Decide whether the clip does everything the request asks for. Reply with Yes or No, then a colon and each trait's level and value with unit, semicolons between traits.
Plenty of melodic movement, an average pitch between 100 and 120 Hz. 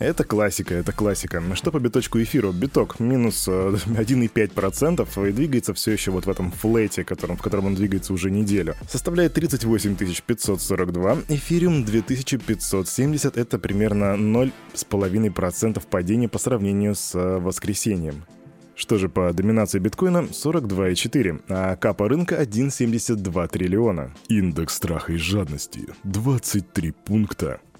No: average, 4.1 semitones; low, 105 Hz